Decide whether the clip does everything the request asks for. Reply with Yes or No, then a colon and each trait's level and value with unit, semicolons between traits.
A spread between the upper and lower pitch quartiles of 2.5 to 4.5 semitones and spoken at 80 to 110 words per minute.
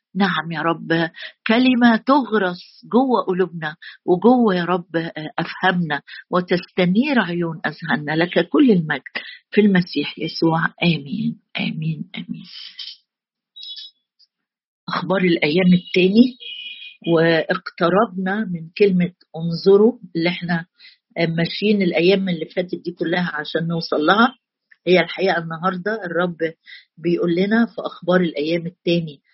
Yes: average, 3.7 semitones; average, 105 wpm